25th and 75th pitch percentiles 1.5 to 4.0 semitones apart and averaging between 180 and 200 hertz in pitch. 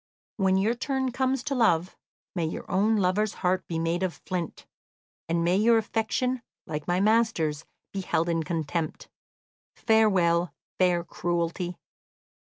No: average, 4.6 semitones; medium, 185 Hz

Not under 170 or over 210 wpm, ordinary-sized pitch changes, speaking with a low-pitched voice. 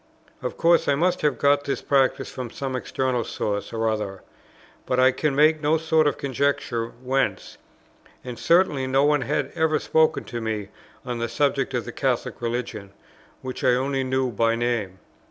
Yes: average, 175 wpm; average, 3.5 semitones; low, 130 Hz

